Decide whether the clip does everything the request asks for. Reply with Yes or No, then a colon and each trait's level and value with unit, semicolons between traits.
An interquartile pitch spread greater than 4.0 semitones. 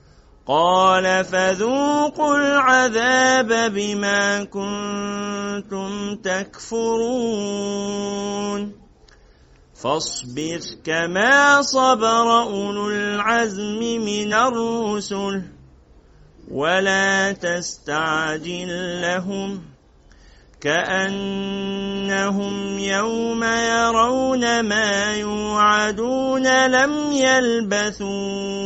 No: average, 3.0 semitones